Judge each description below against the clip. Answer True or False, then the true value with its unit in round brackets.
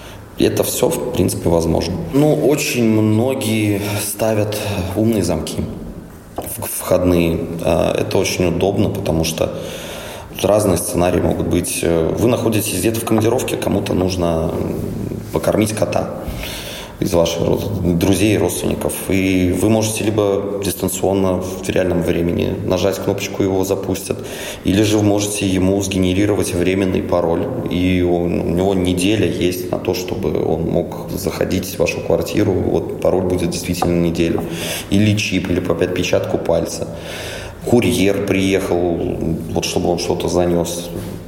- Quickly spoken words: False (135 wpm)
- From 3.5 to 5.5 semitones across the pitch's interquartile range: False (2.8 semitones)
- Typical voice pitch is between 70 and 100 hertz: True (90 Hz)